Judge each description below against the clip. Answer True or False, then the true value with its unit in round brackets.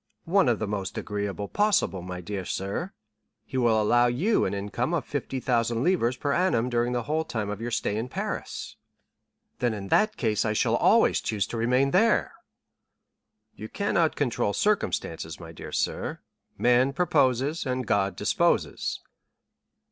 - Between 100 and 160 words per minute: True (155 wpm)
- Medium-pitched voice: False (120 Hz)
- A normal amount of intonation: False (5.8 semitones)